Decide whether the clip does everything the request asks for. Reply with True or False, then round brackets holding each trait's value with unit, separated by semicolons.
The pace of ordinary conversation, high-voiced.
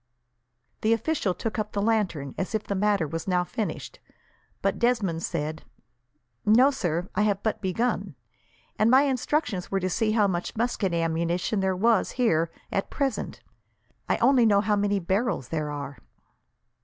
True (160 wpm; 200 Hz)